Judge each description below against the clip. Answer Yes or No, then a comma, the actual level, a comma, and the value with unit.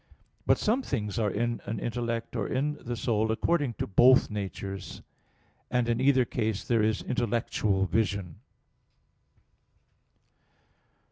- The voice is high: No, low, 115 Hz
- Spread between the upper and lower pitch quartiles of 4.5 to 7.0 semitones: No, average, 2.9 semitones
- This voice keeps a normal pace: No, slow, 125 wpm